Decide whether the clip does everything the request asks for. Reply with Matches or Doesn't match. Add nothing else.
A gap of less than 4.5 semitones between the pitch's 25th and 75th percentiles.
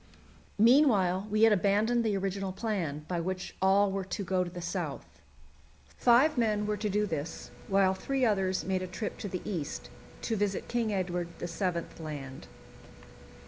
Matches